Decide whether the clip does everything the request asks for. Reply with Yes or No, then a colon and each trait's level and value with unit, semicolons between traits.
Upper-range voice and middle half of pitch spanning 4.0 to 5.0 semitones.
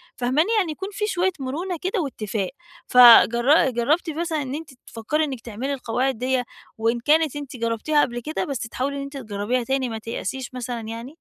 Yes: very high, 260 Hz; average, 4.5 semitones